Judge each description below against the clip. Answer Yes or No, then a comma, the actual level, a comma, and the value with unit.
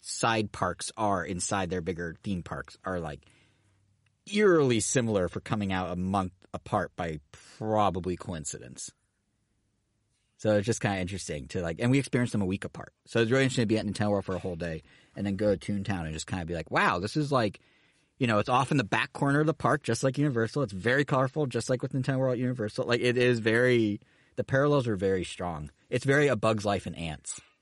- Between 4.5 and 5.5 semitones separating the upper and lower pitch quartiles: Yes, average, 4.8 semitones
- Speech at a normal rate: No, fast, 225 wpm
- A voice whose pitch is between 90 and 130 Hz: Yes, low, 105 Hz